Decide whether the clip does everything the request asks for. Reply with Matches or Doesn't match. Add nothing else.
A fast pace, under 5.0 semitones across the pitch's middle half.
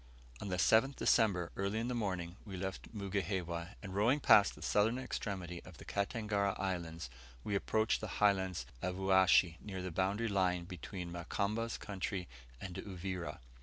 Doesn't match